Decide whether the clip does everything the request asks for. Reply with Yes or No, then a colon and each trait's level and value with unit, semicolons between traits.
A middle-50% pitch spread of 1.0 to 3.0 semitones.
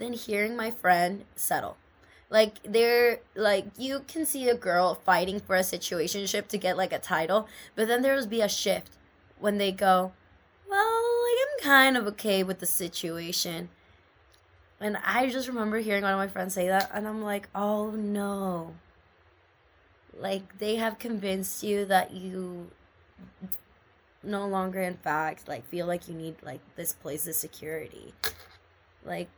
No: average, 3.7 semitones